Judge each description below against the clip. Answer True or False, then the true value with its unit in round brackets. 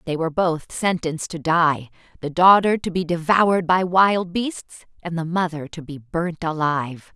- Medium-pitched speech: True (170 Hz)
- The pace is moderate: True (170 wpm)